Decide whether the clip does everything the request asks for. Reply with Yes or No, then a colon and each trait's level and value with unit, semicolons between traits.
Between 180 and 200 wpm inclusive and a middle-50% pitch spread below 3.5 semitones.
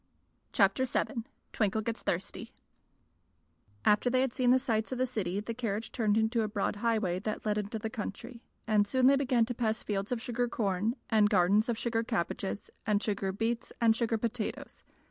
Yes: average, 185 wpm; narrow, 2.5 semitones